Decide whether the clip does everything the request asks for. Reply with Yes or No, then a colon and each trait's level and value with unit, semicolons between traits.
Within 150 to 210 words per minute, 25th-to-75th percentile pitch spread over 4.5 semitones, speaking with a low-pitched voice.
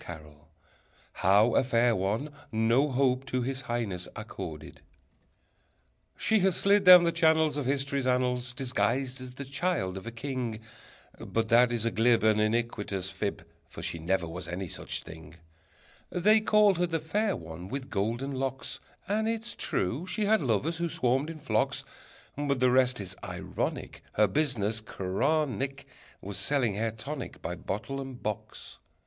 Yes: average, 160 wpm; average, 5.2 semitones; low, 125 Hz